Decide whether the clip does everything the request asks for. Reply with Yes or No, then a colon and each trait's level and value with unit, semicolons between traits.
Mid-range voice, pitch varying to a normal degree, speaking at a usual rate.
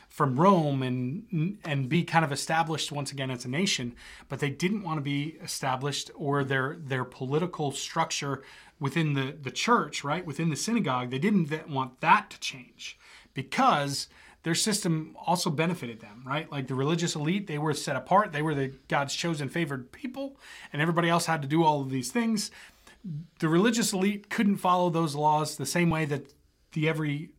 Yes: medium, 155 Hz; average, 3.6 semitones; average, 185 wpm